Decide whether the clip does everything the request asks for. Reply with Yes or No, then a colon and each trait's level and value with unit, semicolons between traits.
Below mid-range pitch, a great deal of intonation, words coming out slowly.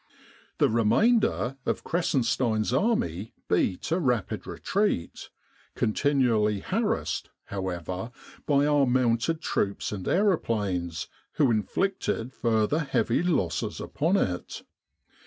Yes: low, 120 Hz; wide, 6.4 semitones; slow, 100 wpm